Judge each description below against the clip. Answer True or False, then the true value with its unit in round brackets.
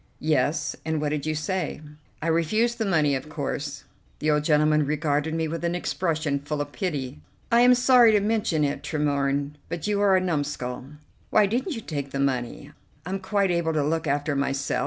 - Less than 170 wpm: False (195 wpm)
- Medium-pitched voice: True (155 Hz)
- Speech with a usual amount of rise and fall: True (4.3 semitones)